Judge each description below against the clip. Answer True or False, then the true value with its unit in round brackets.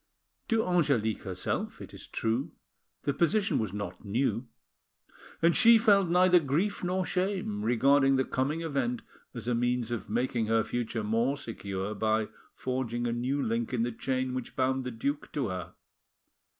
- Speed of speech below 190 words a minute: True (165 wpm)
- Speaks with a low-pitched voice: True (125 Hz)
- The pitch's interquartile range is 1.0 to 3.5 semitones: False (4.6 semitones)